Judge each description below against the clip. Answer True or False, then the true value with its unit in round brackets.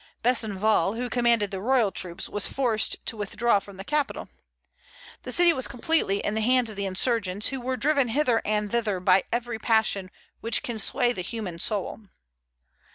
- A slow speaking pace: False (175 wpm)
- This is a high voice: True (225 Hz)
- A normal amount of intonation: True (3.5 semitones)